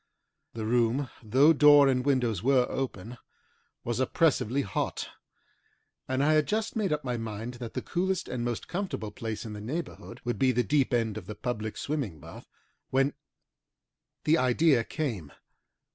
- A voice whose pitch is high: No, low, 125 Hz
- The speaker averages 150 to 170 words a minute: Yes, average, 160 wpm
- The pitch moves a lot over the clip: No, average, 4.4 semitones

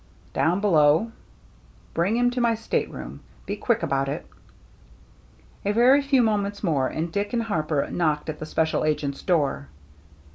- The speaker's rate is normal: Yes, average, 160 wpm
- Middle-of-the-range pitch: Yes, medium, 170 Hz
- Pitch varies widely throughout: Yes, wide, 6.9 semitones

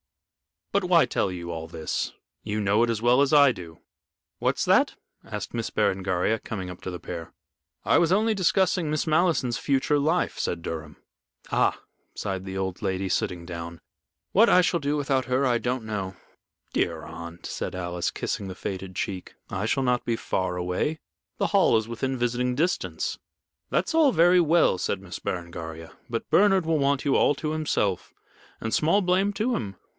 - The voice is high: No, low, 115 Hz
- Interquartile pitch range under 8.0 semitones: No, wide, 9.0 semitones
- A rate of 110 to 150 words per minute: No, average, 180 wpm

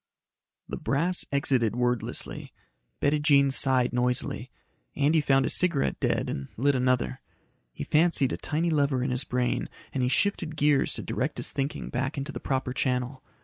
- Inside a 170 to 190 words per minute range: No, average, 160 wpm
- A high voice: No, low, 135 Hz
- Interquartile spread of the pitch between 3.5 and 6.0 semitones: No, average, 2.7 semitones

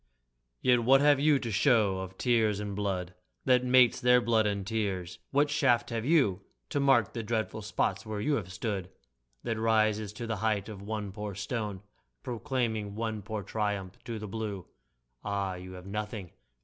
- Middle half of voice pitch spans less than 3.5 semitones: Yes, average, 2.9 semitones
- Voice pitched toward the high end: No, low, 110 Hz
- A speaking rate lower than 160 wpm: No, average, 175 wpm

